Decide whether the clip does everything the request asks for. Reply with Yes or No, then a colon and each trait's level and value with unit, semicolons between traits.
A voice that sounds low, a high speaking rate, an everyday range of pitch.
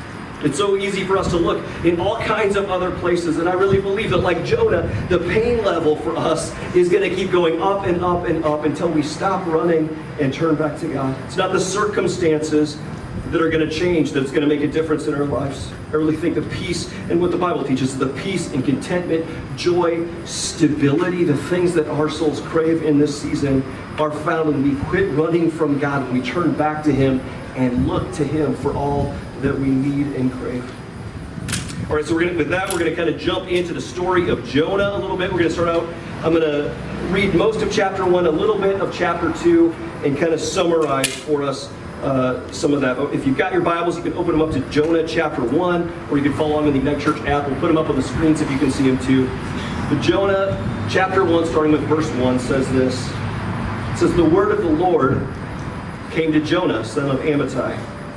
No: medium, 155 Hz; fast, 225 wpm; average, 3.6 semitones